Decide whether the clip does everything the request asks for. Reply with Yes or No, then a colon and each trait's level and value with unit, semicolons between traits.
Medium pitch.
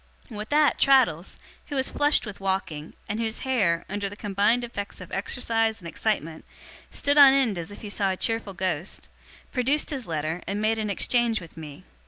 No: high, 210 Hz